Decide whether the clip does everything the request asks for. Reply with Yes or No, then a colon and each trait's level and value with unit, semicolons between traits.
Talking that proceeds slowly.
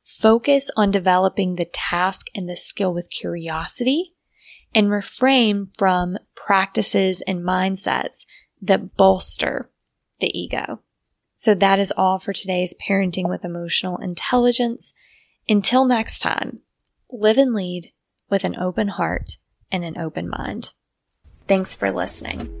Yes: slow, 125 wpm